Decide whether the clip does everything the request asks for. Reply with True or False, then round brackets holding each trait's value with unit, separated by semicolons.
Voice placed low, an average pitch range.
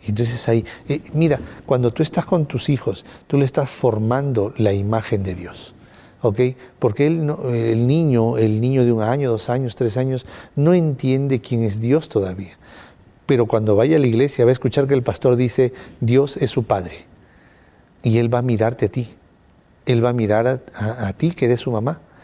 True (125 Hz; 3.3 semitones)